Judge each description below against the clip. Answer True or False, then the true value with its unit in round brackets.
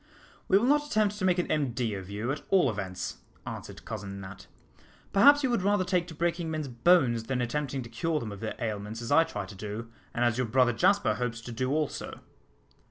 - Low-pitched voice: True (130 Hz)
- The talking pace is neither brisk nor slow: False (220 wpm)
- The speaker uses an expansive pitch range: True (7.7 semitones)